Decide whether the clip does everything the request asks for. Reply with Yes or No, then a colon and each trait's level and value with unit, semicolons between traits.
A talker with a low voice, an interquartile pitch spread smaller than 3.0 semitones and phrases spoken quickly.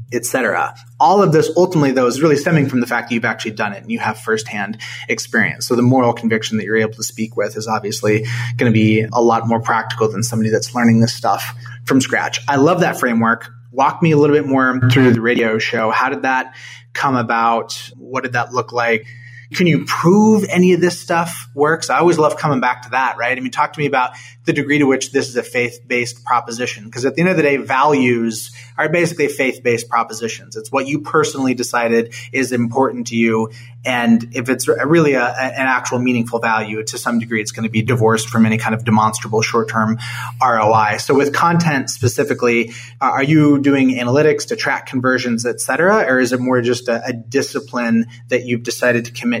Yes: low, 120 Hz; narrow, 2.6 semitones; fast, 215 wpm